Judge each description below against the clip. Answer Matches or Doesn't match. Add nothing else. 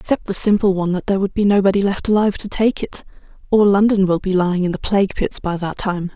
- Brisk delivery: Matches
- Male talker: Doesn't match